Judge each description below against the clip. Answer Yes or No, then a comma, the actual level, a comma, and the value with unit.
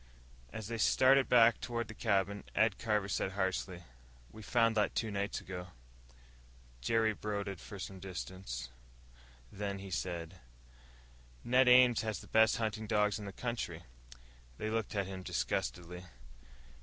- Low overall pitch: Yes, low, 105 Hz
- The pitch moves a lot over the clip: No, average, 3.0 semitones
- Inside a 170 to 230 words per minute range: No, average, 145 wpm